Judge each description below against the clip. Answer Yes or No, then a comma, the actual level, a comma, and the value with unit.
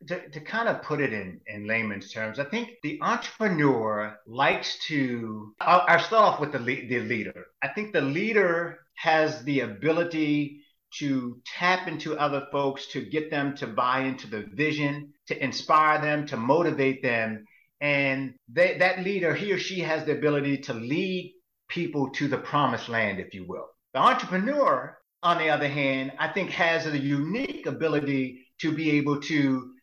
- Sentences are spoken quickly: No, average, 175 wpm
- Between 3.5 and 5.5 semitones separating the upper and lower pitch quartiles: Yes, average, 4.2 semitones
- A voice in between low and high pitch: Yes, medium, 145 Hz